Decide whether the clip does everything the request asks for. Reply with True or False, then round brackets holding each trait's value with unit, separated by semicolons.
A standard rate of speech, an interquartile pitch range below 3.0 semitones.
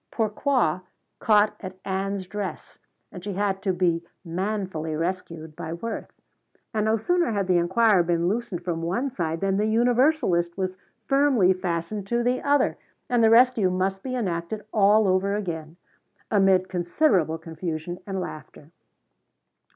False (145 wpm; 4.0 semitones)